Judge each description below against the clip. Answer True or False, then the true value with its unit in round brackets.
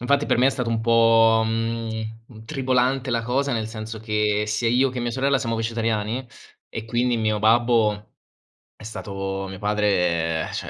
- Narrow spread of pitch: True (2.1 semitones)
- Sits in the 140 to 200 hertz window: False (115 Hz)